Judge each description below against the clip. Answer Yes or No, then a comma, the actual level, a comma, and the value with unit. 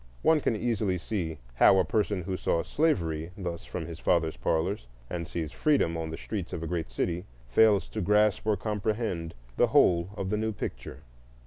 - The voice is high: No, very low, 90 Hz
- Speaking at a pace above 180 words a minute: Yes, average, 190 wpm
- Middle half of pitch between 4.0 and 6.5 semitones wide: Yes, average, 4.3 semitones